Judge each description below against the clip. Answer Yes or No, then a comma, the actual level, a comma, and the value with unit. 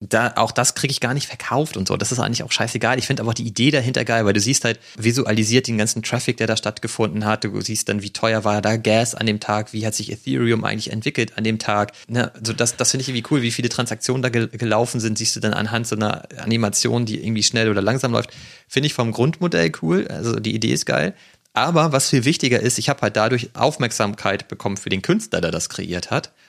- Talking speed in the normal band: No, fast, 255 wpm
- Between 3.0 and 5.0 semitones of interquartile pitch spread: No, narrow, 2.6 semitones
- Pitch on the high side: No, low, 115 Hz